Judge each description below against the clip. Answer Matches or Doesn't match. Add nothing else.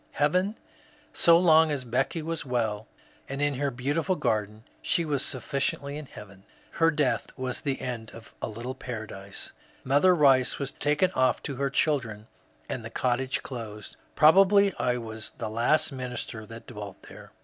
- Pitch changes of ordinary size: Matches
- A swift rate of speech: Doesn't match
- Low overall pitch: Matches